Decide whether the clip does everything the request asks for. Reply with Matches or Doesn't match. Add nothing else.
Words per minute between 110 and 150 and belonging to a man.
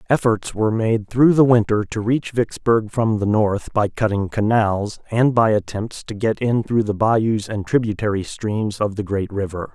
Doesn't match